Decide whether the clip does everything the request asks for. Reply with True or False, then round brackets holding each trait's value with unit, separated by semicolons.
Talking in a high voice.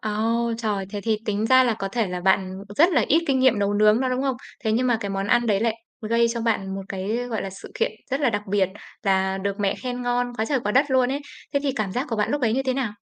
True (225 Hz)